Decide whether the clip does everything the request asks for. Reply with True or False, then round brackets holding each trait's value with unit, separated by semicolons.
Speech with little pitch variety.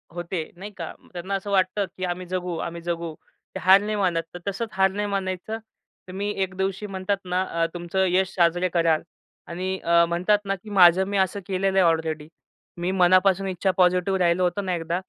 True (1.9 semitones)